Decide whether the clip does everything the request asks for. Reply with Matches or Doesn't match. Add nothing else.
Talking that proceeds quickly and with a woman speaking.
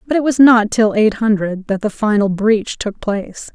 Matches